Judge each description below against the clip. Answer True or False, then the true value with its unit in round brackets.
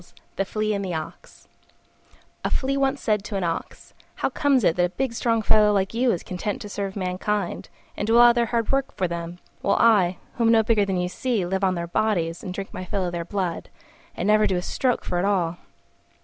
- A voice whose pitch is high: True (200 Hz)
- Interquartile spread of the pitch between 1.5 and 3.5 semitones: False (4.1 semitones)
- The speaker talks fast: True (235 wpm)